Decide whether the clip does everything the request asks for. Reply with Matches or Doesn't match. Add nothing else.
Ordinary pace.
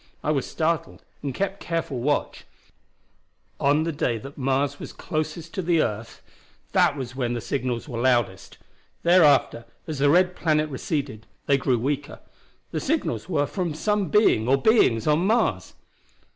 Matches